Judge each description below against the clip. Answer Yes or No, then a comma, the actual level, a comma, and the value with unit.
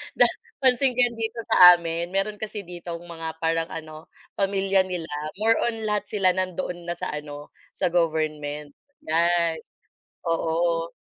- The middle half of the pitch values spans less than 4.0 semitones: Yes, average, 3.1 semitones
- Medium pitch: Yes, medium, 175 Hz